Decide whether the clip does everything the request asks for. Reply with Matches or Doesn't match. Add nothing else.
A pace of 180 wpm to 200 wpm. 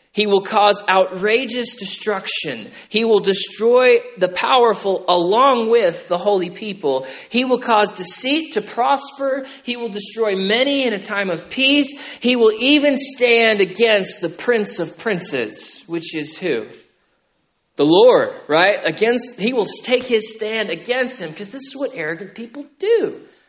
Doesn't match